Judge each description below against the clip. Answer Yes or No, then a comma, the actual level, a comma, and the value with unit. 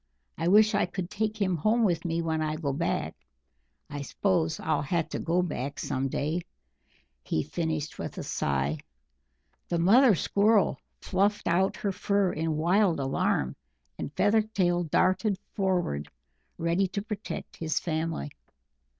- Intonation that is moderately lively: Yes, average, 4.2 semitones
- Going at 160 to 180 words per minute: No, average, 145 wpm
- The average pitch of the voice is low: No, medium, 175 Hz